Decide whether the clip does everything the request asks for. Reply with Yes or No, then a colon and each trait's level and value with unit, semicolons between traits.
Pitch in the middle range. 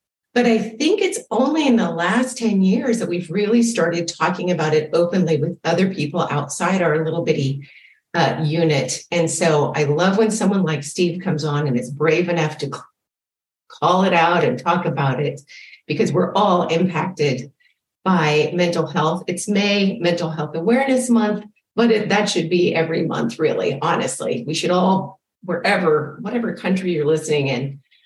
Yes: medium, 175 Hz